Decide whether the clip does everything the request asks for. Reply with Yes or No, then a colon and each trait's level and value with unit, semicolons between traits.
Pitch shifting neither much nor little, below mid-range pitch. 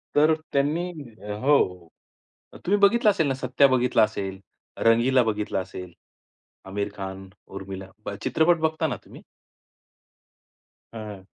No: wide, 7.4 semitones; low, 120 Hz